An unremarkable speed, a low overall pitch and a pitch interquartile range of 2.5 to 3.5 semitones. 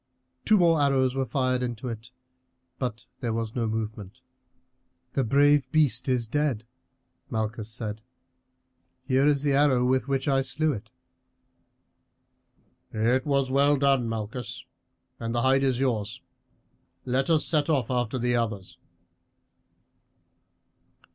No: slow, 130 wpm; low, 130 Hz; average, 3.2 semitones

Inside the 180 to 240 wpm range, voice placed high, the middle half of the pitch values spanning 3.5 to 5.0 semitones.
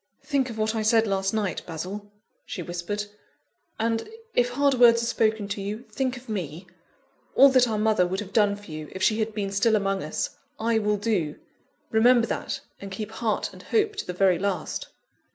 No: average, 200 wpm; high, 215 Hz; average, 2.9 semitones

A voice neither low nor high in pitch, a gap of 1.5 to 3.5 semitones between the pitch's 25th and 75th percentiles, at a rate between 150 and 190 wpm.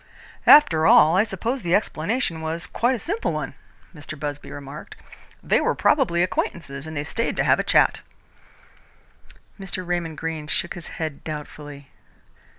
No: medium, 165 Hz; average, 4.3 semitones; average, 155 wpm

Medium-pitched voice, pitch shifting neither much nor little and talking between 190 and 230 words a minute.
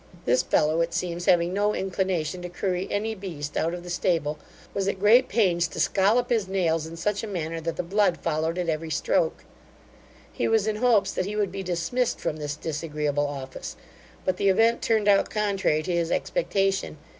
Yes: medium, 180 Hz; average, 3.8 semitones; average, 195 wpm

